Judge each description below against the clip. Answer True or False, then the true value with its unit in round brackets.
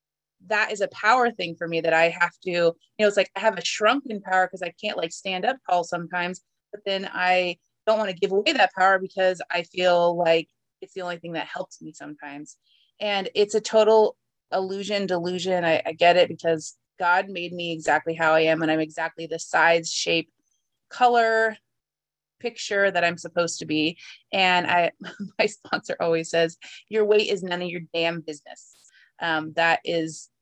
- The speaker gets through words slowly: False (195 wpm)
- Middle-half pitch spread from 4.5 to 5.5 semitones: False (3.2 semitones)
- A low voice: False (175 Hz)